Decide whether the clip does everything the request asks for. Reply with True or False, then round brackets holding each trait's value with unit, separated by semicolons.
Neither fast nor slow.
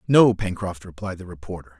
True (165 wpm)